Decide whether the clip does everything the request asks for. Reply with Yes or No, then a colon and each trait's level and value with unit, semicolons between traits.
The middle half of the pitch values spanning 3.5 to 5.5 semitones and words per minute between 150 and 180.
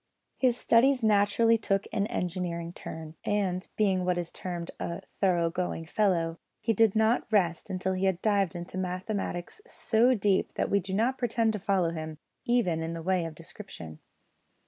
Yes: average, 3.8 semitones; average, 170 wpm